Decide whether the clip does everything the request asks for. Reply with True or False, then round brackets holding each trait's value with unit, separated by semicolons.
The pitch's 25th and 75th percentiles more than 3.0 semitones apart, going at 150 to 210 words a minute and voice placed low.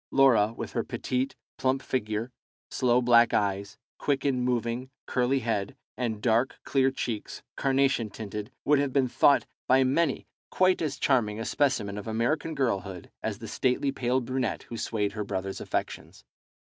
True (3.8 semitones; 160 wpm; 125 Hz)